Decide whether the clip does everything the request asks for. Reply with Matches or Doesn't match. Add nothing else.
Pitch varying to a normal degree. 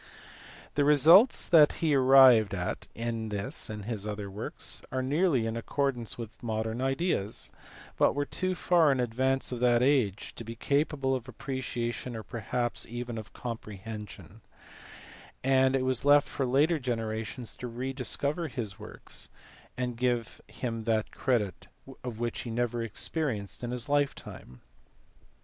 Matches